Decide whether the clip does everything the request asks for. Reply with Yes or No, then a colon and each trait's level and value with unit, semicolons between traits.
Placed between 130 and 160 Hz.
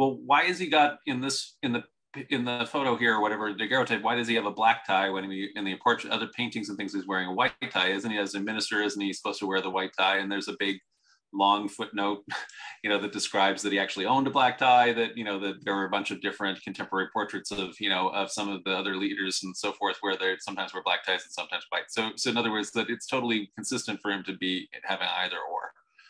No: low, 100 Hz